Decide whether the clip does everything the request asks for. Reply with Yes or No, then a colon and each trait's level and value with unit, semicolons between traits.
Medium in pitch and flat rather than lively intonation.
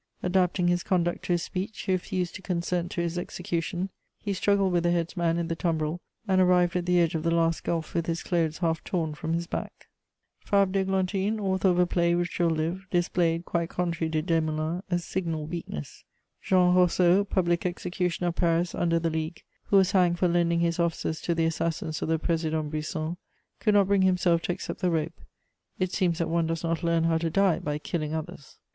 Yes: medium, 170 Hz; narrow, 1.6 semitones